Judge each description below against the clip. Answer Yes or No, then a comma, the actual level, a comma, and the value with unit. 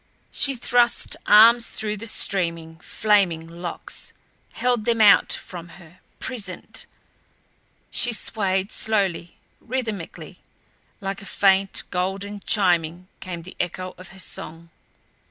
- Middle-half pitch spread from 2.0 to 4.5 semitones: Yes, average, 3.7 semitones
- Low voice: No, high, 195 Hz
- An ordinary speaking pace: No, slow, 115 wpm